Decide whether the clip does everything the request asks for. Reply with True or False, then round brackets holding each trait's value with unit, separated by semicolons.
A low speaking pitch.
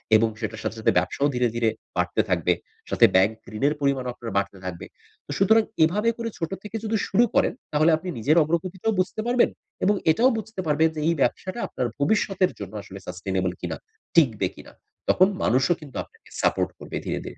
False (150 Hz)